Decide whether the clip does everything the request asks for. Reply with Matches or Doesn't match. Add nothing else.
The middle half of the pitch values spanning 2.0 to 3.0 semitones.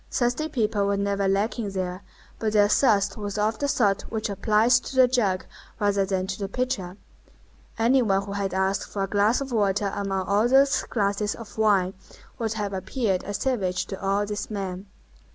Matches